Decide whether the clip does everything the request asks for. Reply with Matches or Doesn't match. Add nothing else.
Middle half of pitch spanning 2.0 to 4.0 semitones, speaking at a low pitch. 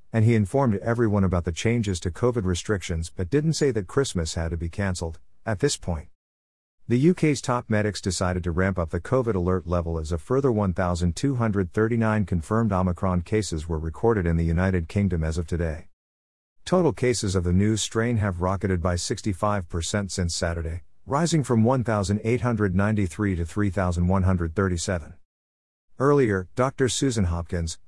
Doesn't match